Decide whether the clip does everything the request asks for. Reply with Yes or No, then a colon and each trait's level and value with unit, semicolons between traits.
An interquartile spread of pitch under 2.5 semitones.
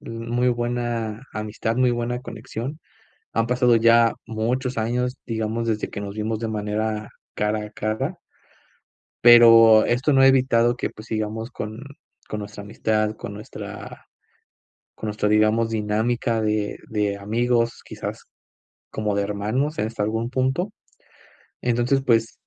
Yes: narrow, 2.0 semitones